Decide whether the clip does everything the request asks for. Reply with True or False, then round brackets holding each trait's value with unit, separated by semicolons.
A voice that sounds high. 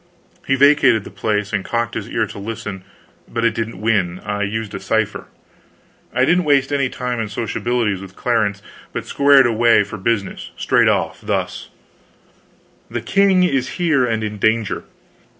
False (115 Hz)